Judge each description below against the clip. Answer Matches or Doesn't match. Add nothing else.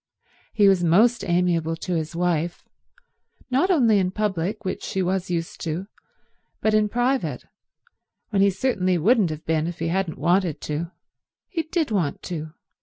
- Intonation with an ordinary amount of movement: Matches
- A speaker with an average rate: Matches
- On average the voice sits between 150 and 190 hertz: Matches